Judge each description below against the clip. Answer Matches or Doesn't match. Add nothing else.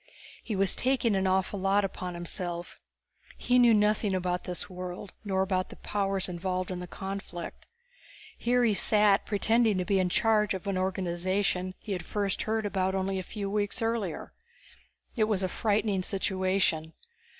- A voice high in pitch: Matches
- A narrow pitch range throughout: Matches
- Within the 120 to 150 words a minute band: Doesn't match